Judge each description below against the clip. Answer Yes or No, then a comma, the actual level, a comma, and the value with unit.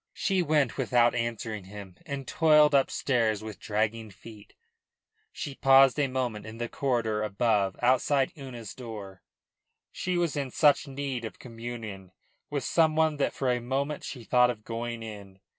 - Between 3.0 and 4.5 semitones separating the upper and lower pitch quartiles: Yes, average, 4.1 semitones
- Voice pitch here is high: No, low, 120 Hz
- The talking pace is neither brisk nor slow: Yes, average, 160 wpm